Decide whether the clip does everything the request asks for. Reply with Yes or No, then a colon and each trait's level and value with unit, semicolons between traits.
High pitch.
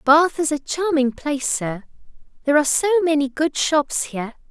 Yes: very high, 295 Hz